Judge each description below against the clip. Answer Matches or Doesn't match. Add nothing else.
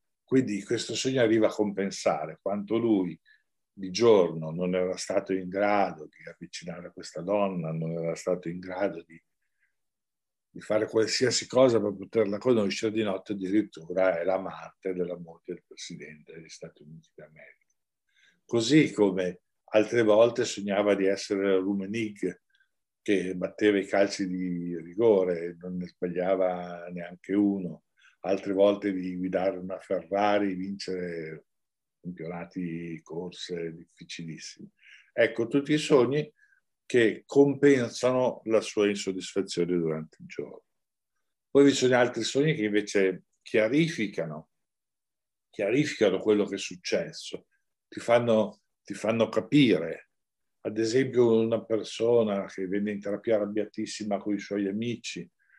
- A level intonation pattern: Doesn't match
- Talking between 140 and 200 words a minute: Doesn't match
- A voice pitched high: Doesn't match